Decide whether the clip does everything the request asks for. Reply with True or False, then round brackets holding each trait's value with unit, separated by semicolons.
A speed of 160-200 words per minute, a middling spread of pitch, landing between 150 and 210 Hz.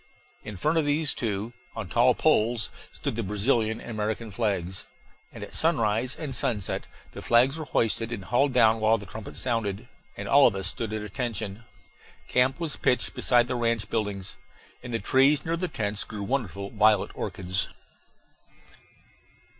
False (165 wpm; 3.6 semitones; 115 Hz)